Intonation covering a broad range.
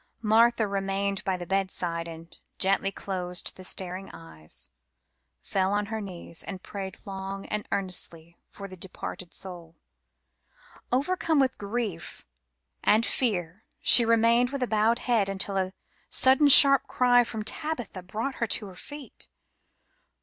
No: average, 4.1 semitones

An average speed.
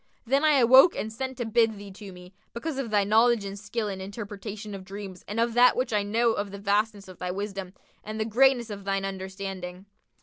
No: fast, 230 wpm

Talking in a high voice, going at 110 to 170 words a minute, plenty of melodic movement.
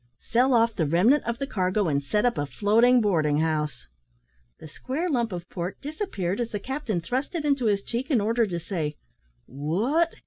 No: high, 215 Hz; average, 195 wpm; wide, 6.8 semitones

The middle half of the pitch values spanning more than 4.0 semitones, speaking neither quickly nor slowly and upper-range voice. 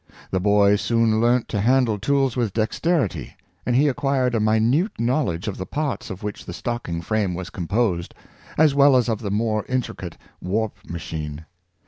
No: average, 4.4 semitones; average, 170 wpm; low, 110 Hz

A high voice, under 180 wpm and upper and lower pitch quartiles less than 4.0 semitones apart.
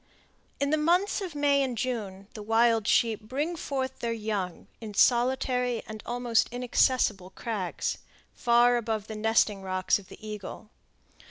Yes: high, 230 Hz; average, 150 wpm; average, 3.3 semitones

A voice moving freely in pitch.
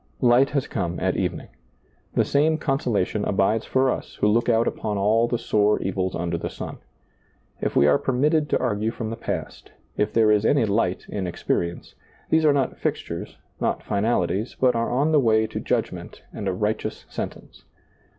No: average, 4.2 semitones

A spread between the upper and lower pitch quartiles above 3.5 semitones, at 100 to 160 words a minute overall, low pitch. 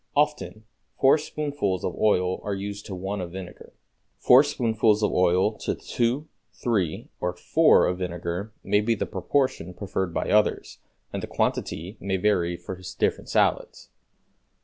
Yes: average, 4.0 semitones; average, 150 wpm; low, 100 Hz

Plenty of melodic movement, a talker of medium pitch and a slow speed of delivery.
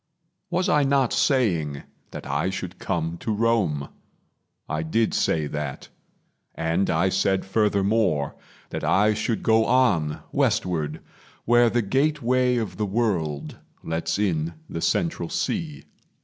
No: wide, 6.6 semitones; low, 100 Hz; slow, 130 wpm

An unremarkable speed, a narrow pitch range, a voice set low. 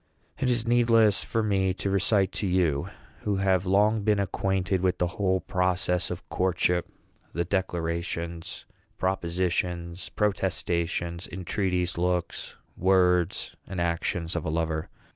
No: slow, 125 wpm; narrow, 2.1 semitones; very low, 90 Hz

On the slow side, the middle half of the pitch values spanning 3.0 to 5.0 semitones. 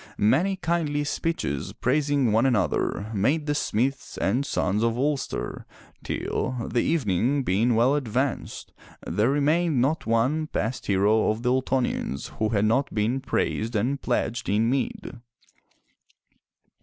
Yes: slow, 130 wpm; average, 4.6 semitones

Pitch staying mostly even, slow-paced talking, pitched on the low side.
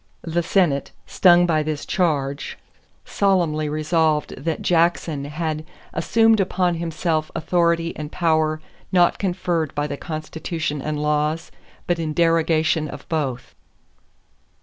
No: narrow, 2.1 semitones; slow, 120 wpm; medium, 160 Hz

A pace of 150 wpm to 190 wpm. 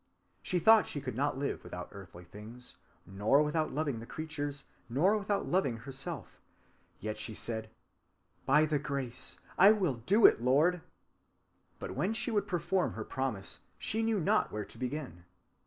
Yes: average, 160 wpm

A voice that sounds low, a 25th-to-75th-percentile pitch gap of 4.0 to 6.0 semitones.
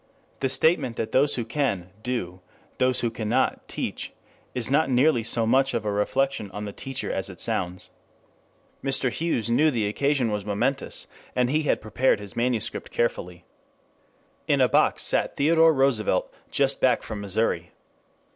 Yes: low, 120 Hz; average, 4.3 semitones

